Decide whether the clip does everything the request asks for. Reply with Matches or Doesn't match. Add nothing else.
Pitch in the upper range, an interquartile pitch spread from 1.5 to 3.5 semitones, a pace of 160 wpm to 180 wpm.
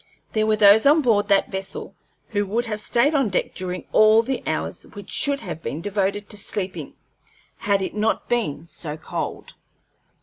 Matches